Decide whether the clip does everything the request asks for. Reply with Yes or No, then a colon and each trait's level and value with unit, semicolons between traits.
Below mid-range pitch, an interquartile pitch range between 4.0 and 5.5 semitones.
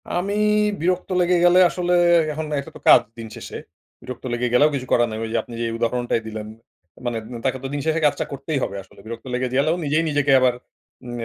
Yes: low, 130 Hz; average, 4.7 semitones